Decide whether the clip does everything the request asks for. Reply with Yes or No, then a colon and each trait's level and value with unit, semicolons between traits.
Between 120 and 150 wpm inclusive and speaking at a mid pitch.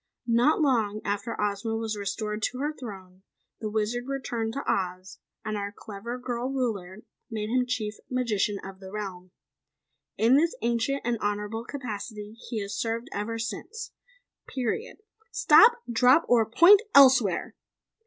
No: average, 145 wpm; high, 225 Hz